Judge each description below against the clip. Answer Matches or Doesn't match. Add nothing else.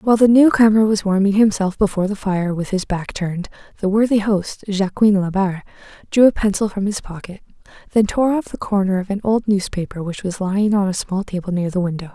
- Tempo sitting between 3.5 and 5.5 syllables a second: Doesn't match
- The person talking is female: Matches